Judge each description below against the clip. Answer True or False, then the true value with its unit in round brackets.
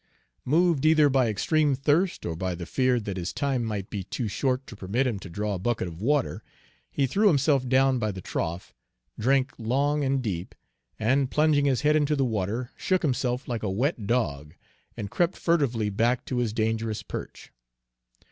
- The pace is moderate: True (185 wpm)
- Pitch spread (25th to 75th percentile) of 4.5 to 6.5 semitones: True (5.0 semitones)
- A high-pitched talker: False (125 Hz)